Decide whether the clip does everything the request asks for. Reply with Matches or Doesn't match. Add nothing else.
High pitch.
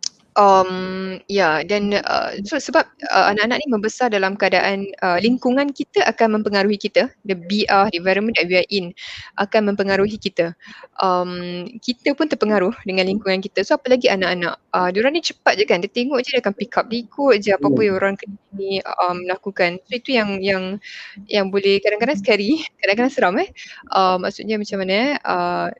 Matches